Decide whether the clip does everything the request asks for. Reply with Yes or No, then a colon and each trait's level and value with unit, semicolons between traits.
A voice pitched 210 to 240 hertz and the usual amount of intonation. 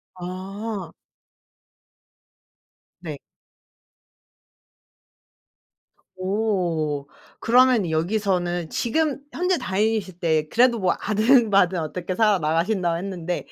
No: high, 190 Hz; average, 4.2 semitones